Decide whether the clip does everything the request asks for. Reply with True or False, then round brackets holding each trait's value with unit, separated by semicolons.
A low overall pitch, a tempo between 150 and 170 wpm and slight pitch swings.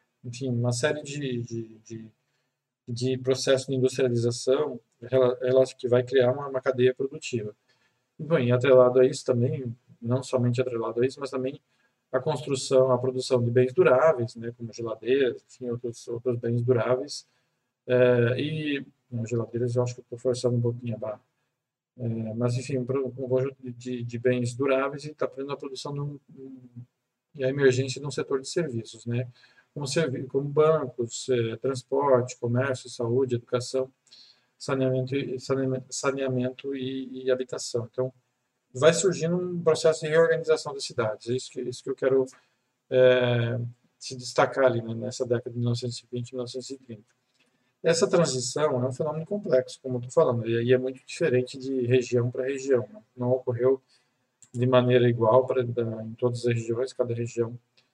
True (125 Hz; 160 wpm; 1.3 semitones)